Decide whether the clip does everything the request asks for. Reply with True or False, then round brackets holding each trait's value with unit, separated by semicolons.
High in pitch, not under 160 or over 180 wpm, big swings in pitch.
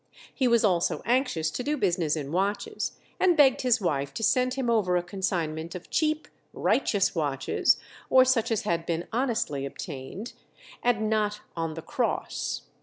True (205 Hz; 165 wpm; 6.9 semitones)